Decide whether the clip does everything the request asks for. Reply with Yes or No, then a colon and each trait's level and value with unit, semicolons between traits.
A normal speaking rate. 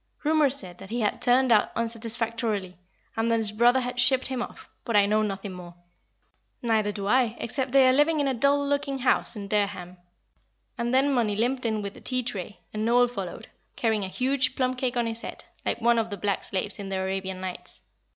No: fast, 215 wpm